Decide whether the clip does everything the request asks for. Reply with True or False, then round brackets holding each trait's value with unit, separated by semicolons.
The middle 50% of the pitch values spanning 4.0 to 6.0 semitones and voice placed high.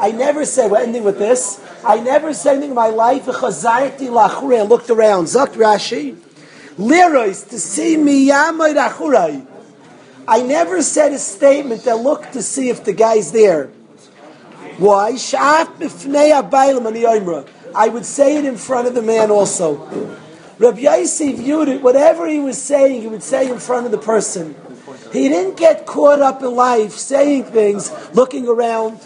True (4.4 semitones; 250 Hz)